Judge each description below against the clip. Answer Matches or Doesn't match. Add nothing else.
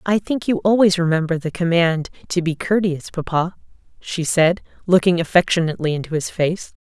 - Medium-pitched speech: Matches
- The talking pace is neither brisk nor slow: Matches